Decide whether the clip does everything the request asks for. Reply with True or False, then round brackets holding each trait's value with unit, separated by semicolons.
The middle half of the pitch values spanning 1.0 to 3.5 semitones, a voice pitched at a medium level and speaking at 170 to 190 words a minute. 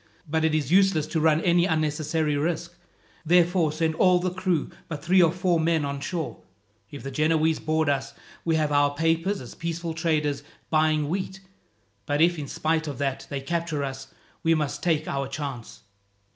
True (2.6 semitones; 160 Hz; 180 wpm)